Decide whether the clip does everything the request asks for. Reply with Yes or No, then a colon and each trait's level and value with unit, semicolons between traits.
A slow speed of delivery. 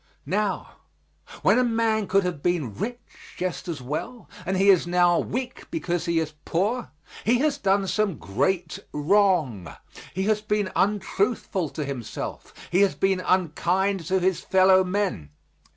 No: average, 150 wpm